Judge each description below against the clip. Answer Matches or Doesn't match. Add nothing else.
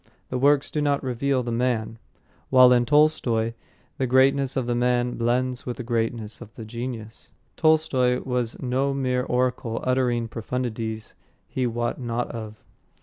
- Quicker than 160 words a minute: Doesn't match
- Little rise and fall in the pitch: Matches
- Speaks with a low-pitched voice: Matches